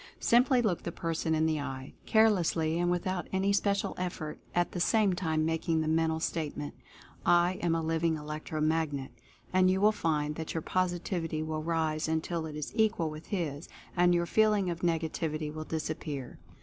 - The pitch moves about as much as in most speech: No, narrow, 2.3 semitones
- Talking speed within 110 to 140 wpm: No, average, 180 wpm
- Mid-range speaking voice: Yes, medium, 165 Hz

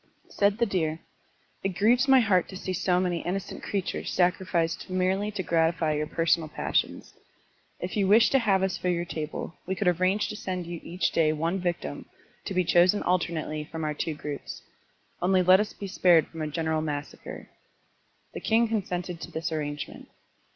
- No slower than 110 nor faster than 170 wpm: No, average, 180 wpm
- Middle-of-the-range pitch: Yes, medium, 180 Hz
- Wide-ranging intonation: No, average, 2.9 semitones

